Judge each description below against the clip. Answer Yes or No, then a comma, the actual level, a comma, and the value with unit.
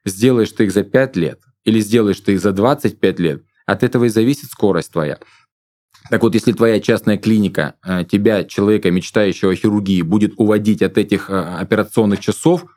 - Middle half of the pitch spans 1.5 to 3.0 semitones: Yes, average, 2.7 semitones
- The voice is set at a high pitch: No, low, 105 Hz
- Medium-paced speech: No, fast, 170 wpm